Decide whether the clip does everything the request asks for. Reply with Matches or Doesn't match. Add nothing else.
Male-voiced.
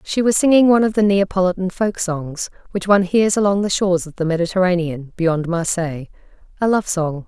Doesn't match